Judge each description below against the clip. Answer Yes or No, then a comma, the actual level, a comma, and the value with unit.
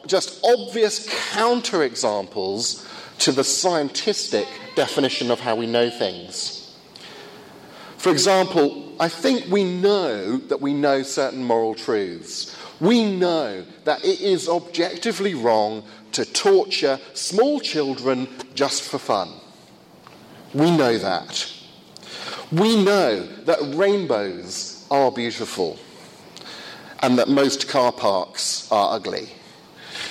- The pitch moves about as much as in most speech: No, wide, 7.6 semitones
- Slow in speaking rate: Yes, slow, 110 wpm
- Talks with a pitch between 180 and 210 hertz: No, medium, 170 Hz